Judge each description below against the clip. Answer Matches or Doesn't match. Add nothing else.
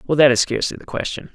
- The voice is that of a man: Matches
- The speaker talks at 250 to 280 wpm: Matches